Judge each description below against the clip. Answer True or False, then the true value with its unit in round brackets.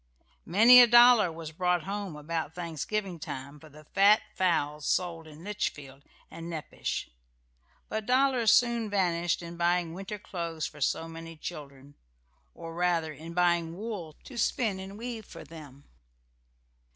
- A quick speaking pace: False (145 wpm)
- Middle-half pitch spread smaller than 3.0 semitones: False (4.3 semitones)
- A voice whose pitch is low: False (170 Hz)